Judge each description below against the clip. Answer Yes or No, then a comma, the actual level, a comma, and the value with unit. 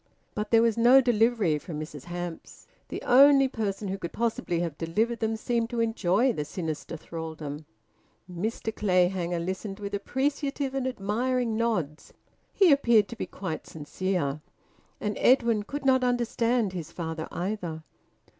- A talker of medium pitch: No, high, 210 Hz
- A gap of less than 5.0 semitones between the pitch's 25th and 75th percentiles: No, wide, 5.6 semitones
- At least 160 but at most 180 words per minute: No, average, 145 wpm